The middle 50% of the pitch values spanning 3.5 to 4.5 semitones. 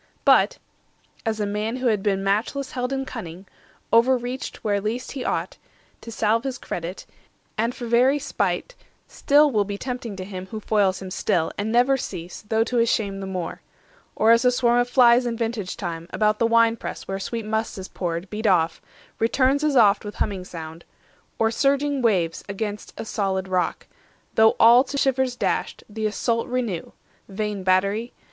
Yes: average, 3.9 semitones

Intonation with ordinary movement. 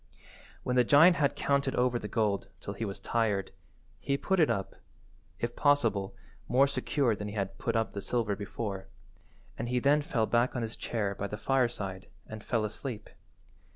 Yes: average, 4.6 semitones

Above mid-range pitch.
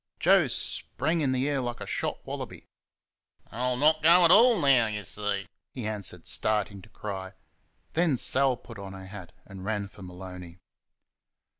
No: low, 110 Hz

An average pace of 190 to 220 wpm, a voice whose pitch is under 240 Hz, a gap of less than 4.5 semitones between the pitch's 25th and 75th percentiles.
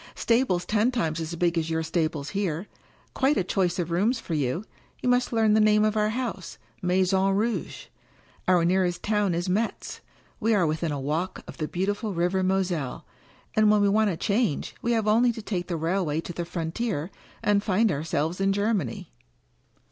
Yes: average, 195 wpm; high, 190 Hz; average, 4.1 semitones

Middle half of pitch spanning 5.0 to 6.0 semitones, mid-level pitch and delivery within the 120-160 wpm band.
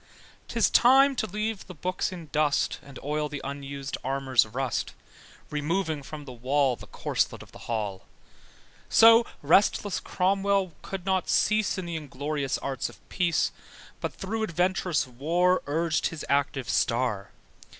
Yes: wide, 5.4 semitones; medium, 155 Hz; average, 145 wpm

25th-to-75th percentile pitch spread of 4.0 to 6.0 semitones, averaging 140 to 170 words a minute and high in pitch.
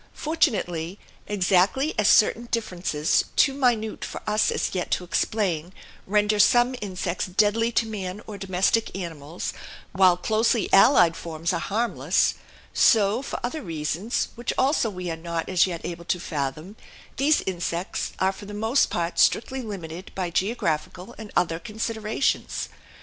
Yes: average, 4.3 semitones; average, 145 wpm; high, 195 Hz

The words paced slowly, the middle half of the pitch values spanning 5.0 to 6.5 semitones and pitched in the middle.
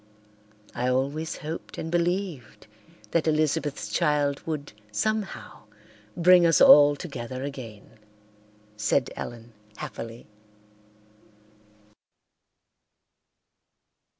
Yes: slow, 75 wpm; average, 5.3 semitones; medium, 145 Hz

